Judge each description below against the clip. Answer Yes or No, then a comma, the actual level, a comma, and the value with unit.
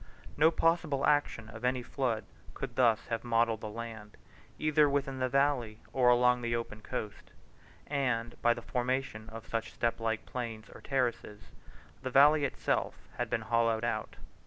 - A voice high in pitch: No, low, 120 Hz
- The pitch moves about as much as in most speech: Yes, average, 3.1 semitones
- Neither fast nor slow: Yes, average, 160 wpm